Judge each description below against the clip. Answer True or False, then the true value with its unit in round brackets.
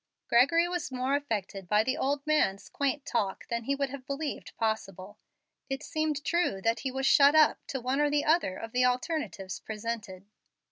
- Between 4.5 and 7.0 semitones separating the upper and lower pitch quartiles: True (4.9 semitones)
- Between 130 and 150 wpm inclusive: False (185 wpm)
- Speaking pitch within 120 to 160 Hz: False (265 Hz)